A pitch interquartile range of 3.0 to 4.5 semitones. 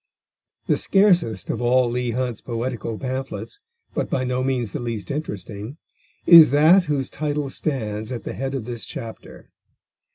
Yes: average, 3.8 semitones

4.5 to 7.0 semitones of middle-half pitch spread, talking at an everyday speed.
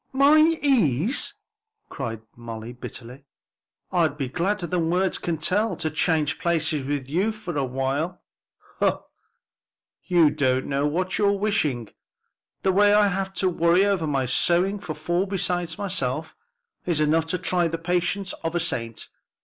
Yes: average, 4.9 semitones; average, 150 wpm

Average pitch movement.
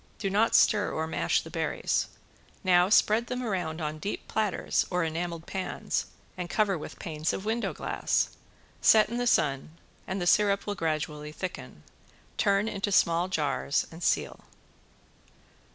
Yes: average, 4.3 semitones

